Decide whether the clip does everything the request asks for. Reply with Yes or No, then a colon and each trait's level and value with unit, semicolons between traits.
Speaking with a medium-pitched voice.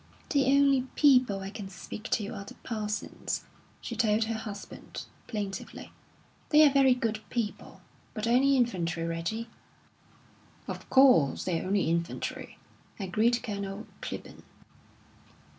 No: high, 215 Hz